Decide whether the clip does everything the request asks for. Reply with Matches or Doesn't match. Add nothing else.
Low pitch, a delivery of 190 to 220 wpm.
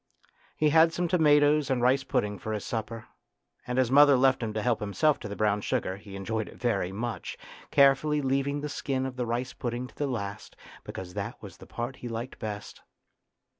Matches